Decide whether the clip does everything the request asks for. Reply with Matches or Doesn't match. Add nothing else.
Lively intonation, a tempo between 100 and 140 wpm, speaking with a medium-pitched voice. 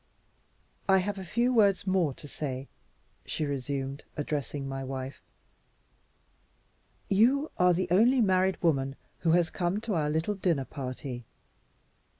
Matches